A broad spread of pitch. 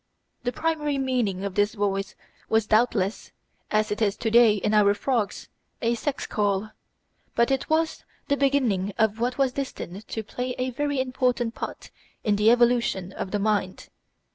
No: average, 3.8 semitones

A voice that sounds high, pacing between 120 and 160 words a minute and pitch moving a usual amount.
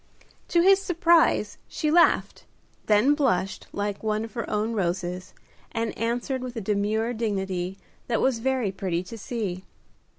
Yes: high, 220 Hz; average, 145 wpm; average, 4.7 semitones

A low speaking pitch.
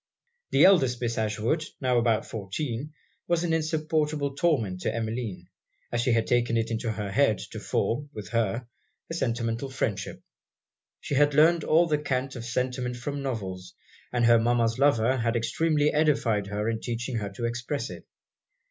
Yes: low, 120 Hz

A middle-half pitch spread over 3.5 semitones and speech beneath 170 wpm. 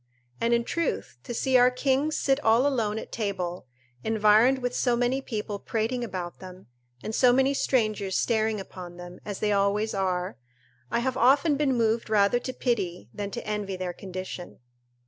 No: average, 4.2 semitones; average, 175 wpm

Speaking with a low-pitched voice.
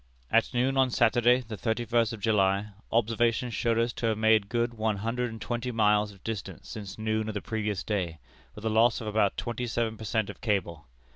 Yes: low, 110 Hz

